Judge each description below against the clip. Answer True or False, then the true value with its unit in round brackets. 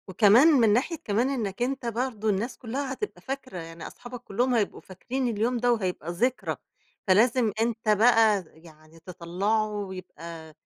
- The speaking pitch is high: True (220 Hz)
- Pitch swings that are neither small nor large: True (4.7 semitones)